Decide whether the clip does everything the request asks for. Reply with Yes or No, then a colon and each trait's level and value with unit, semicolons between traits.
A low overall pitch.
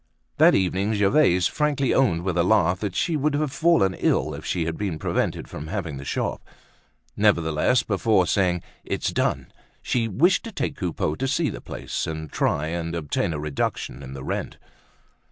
Yes: very low, 95 Hz